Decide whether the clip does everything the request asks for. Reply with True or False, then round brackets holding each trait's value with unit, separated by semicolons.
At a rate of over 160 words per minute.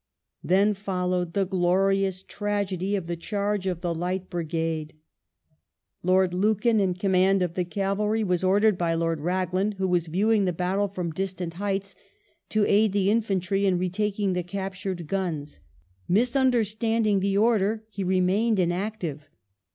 False (150 wpm)